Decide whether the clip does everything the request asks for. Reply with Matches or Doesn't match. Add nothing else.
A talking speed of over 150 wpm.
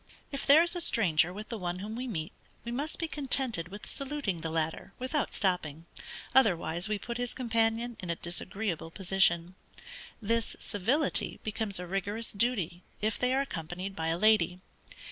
Matches